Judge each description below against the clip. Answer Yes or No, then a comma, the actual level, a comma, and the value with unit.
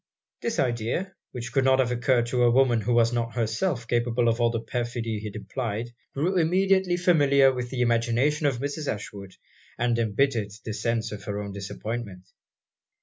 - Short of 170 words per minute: No, average, 175 wpm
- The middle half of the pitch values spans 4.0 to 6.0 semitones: No, average, 3.0 semitones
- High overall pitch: No, low, 120 Hz